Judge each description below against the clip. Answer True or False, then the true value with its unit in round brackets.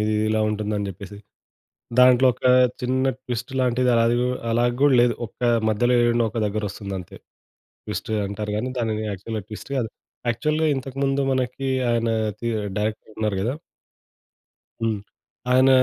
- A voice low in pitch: True (115 Hz)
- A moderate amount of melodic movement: True (3.0 semitones)